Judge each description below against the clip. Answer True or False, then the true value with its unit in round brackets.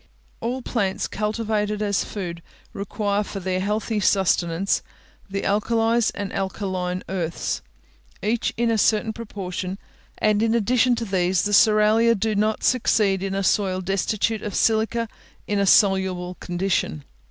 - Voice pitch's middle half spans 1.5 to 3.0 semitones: True (2.6 semitones)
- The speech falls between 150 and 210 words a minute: False (140 wpm)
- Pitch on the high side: True (205 Hz)